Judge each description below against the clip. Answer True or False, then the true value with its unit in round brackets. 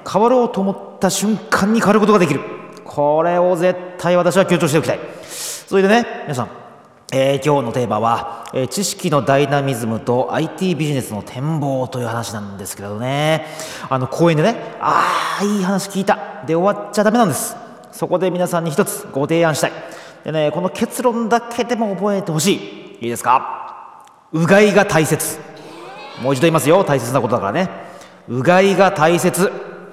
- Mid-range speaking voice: True (170 Hz)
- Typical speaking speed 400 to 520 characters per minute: False (350 characters per minute)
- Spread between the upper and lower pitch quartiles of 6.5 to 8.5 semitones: False (6.1 semitones)